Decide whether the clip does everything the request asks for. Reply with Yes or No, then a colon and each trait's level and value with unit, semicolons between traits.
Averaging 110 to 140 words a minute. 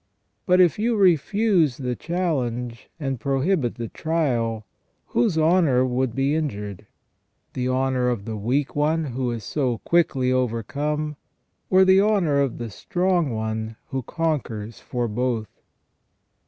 Yes: slow, 135 wpm